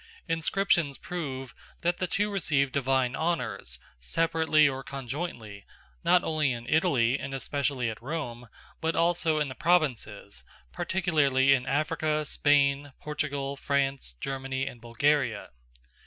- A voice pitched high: No, medium, 140 Hz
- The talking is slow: Yes, slow, 125 wpm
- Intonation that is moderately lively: Yes, average, 3.5 semitones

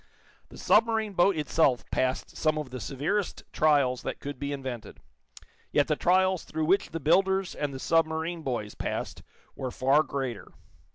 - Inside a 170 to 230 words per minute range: No, average, 160 wpm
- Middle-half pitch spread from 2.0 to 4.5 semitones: No, average, 4.9 semitones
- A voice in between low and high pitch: Yes, medium, 155 Hz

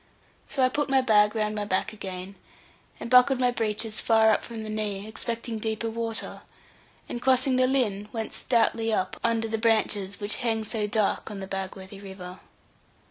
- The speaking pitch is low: No, high, 220 Hz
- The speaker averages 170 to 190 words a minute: Yes, average, 180 wpm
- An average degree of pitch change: No, narrow, 2.2 semitones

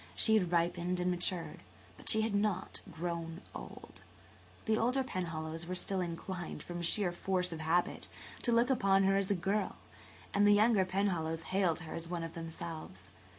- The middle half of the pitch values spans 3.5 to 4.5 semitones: No, average, 3.1 semitones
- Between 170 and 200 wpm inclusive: Yes, average, 175 wpm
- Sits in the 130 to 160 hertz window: No, medium, 180 Hz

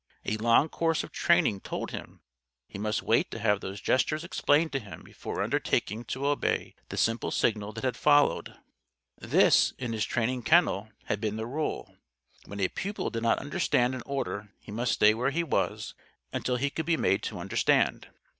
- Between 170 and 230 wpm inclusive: Yes, average, 185 wpm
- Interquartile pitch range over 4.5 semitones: Yes, average, 5.0 semitones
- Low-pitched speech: Yes, low, 120 Hz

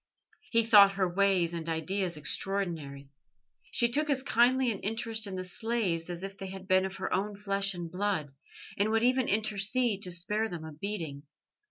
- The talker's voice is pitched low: No, high, 195 Hz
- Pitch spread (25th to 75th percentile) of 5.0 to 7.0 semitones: No, average, 3.9 semitones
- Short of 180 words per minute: No, average, 185 wpm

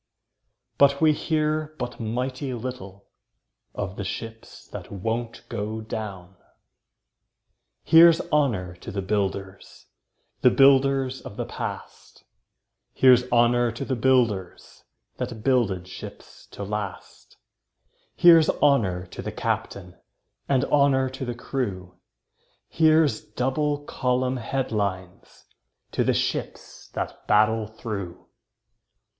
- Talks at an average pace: No, slow, 110 wpm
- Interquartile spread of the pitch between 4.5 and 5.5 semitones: Yes, average, 5.1 semitones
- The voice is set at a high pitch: No, low, 120 Hz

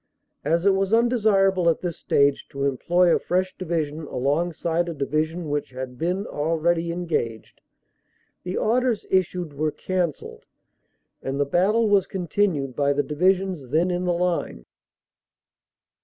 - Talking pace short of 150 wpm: Yes, average, 140 wpm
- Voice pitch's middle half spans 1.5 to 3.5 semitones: No, average, 4.2 semitones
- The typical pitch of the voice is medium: Yes, medium, 170 Hz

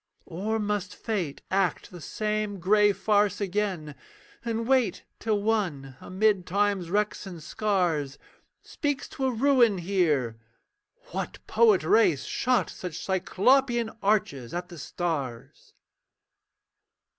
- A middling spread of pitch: Yes, average, 3.9 semitones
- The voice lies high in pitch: Yes, high, 200 Hz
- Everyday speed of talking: No, slow, 115 wpm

